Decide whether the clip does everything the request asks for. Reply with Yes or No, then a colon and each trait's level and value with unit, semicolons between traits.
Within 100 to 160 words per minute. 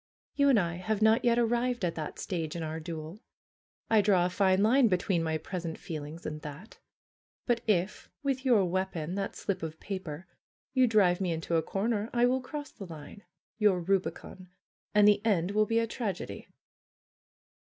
No: average, 185 wpm